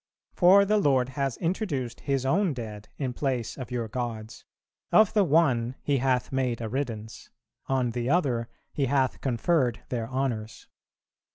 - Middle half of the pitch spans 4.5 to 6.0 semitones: No, average, 3.3 semitones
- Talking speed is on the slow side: No, average, 155 wpm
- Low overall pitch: Yes, low, 130 Hz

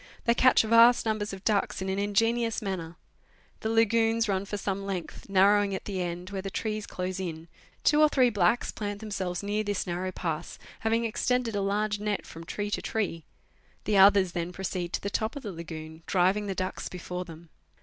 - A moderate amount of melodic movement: Yes, average, 3.0 semitones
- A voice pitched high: Yes, high, 200 Hz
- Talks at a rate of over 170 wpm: Yes, average, 200 wpm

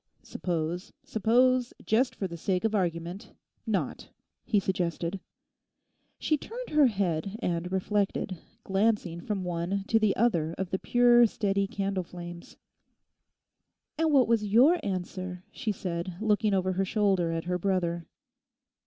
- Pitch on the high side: Yes, high, 195 Hz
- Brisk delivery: No, slow, 135 wpm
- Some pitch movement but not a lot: Yes, average, 3.9 semitones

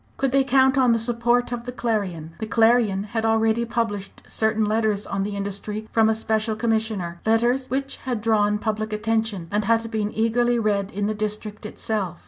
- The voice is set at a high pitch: Yes, high, 220 Hz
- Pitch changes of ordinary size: No, narrow, 2.0 semitones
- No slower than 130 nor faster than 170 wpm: No, average, 185 wpm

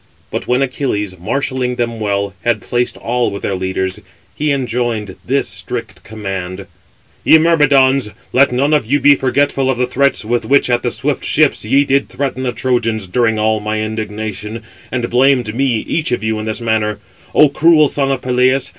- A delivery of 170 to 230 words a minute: Yes, average, 180 wpm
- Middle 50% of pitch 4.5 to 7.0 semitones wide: No, average, 3.9 semitones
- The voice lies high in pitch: No, low, 120 Hz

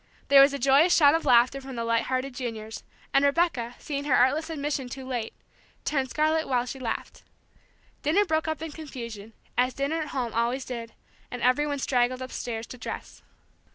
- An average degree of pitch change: Yes, average, 3.3 semitones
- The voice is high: Yes, very high, 265 Hz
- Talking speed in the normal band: Yes, average, 185 wpm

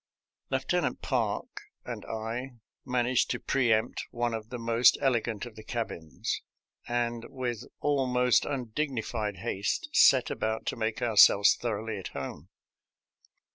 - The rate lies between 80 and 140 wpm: Yes, slow, 135 wpm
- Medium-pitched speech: No, low, 115 Hz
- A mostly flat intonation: Yes, narrow, 2.2 semitones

